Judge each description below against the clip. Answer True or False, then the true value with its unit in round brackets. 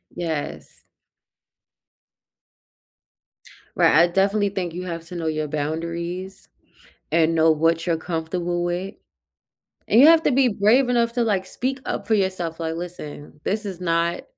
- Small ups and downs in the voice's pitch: False (3.4 semitones)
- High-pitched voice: False (175 Hz)